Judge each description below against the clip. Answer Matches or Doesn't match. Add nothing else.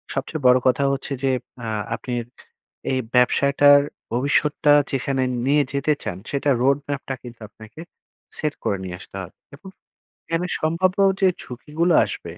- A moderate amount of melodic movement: Matches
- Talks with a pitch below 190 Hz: Matches